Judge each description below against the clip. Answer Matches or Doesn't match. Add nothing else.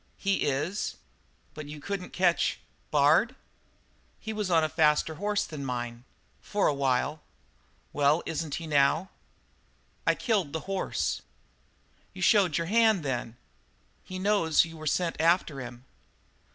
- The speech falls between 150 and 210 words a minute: Doesn't match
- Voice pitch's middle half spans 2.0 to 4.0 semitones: Doesn't match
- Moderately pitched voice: Matches